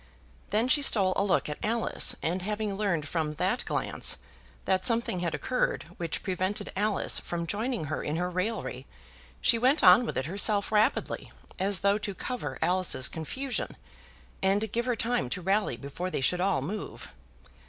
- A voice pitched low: No, high, 195 Hz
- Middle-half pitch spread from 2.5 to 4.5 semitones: Yes, average, 3.9 semitones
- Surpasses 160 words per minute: Yes, average, 170 wpm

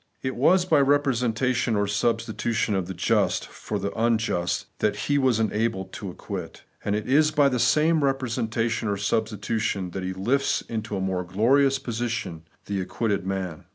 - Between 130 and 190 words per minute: Yes, average, 165 wpm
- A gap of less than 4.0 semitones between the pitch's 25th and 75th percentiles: No, average, 4.6 semitones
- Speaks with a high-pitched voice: No, low, 115 Hz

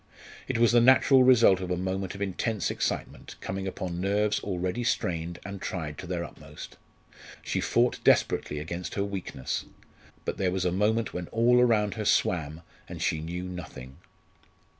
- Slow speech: No, average, 165 wpm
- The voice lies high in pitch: No, very low, 95 Hz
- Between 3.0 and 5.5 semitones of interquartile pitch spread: Yes, average, 3.6 semitones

